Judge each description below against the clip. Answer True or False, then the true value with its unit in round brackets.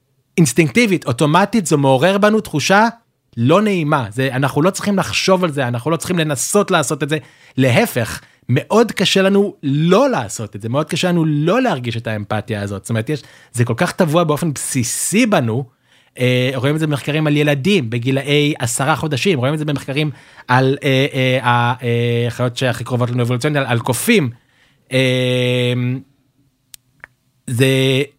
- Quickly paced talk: True (160 wpm)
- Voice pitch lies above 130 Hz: True (140 Hz)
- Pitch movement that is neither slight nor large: True (4.7 semitones)